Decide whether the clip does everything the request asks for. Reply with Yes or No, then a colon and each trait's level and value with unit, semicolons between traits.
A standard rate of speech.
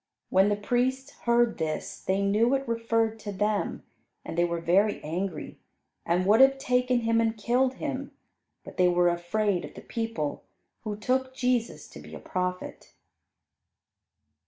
Yes: average, 155 wpm